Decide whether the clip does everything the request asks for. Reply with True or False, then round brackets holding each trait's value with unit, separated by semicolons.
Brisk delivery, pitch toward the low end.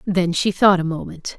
False (215 wpm; 180 Hz)